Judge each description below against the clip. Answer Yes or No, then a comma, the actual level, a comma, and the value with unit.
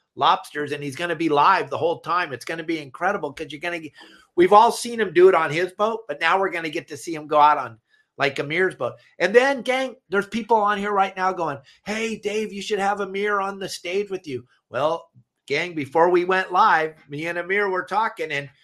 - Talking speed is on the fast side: Yes, fast, 250 wpm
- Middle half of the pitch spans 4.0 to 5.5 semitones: Yes, average, 4.5 semitones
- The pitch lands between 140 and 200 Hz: Yes, medium, 185 Hz